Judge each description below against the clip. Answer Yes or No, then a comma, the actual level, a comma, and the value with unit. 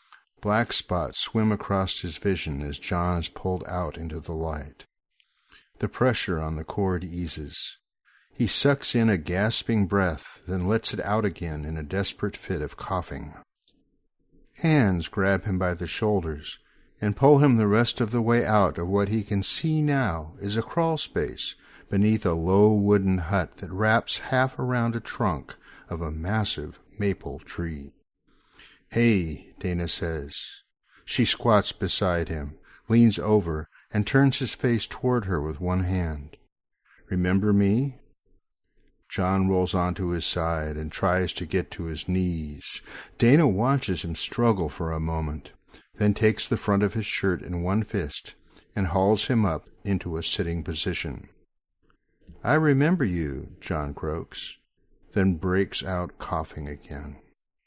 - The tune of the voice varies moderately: Yes, average, 4.5 semitones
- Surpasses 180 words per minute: No, average, 150 wpm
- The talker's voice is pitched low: Yes, very low, 95 Hz